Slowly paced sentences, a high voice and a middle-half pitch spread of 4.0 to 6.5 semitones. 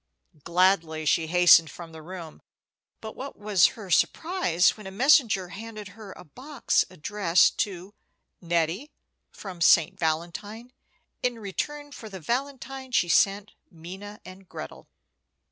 Yes: slow, 130 wpm; high, 195 Hz; average, 4.7 semitones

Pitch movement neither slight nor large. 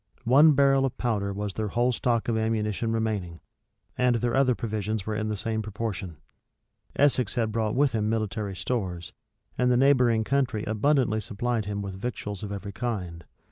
Yes: average, 3.0 semitones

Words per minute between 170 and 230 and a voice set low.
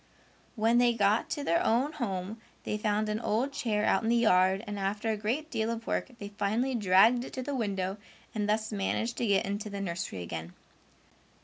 No: fast, 205 wpm; high, 215 Hz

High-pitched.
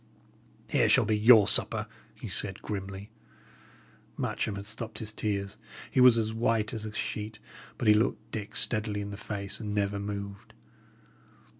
No: low, 105 Hz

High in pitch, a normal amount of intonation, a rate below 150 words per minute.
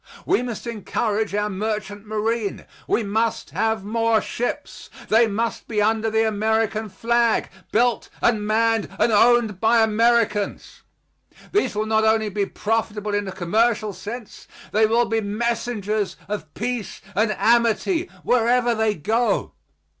No: high, 220 Hz; narrow, 1.7 semitones; average, 140 wpm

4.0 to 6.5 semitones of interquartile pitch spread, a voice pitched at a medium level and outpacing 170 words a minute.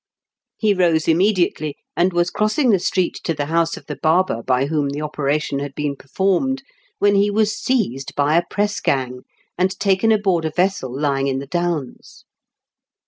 Yes: wide, 5.5 semitones; medium, 170 Hz; average, 180 wpm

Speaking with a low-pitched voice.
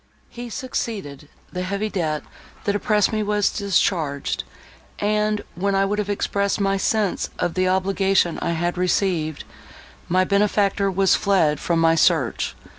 No: high, 195 Hz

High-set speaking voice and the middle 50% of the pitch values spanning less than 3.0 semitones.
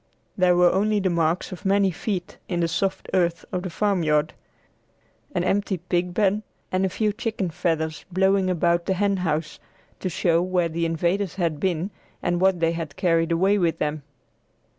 No: medium, 180 Hz; narrow, 2.4 semitones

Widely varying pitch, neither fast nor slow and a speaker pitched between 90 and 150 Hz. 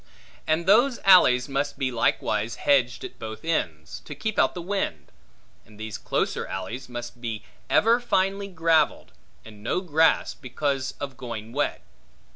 Yes: wide, 7.0 semitones; average, 150 wpm; low, 135 Hz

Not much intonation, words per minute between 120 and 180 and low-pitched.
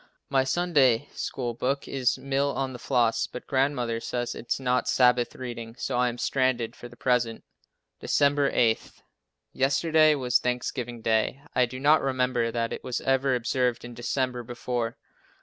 Yes: narrow, 2.0 semitones; average, 165 wpm; low, 125 Hz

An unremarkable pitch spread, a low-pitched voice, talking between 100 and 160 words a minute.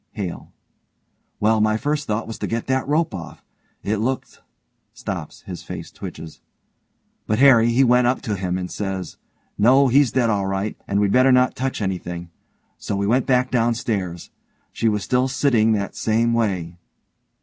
No: average, 4.3 semitones; low, 110 Hz; average, 175 wpm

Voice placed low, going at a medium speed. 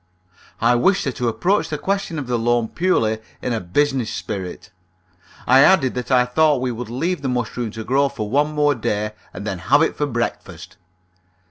Yes: low, 125 Hz; average, 195 wpm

